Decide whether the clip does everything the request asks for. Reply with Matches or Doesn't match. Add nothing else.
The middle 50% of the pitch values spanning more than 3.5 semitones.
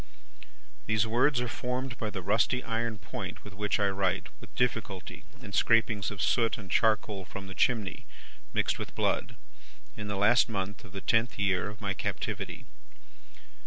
Doesn't match